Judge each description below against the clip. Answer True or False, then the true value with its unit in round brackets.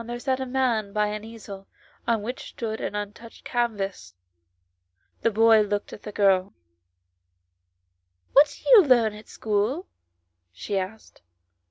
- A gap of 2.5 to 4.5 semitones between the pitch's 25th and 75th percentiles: True (2.9 semitones)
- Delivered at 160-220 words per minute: False (150 wpm)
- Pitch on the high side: True (215 Hz)